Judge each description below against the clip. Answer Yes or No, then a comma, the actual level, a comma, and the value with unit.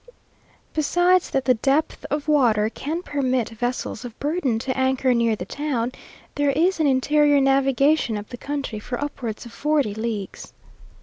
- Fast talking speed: No, average, 160 wpm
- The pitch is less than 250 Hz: No, very high, 265 Hz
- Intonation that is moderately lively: Yes, average, 3.8 semitones